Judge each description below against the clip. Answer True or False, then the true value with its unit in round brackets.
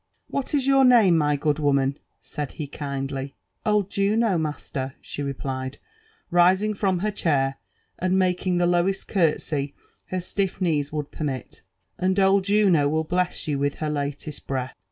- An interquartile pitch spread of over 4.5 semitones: True (5.1 semitones)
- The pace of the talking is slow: False (175 wpm)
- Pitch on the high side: False (160 Hz)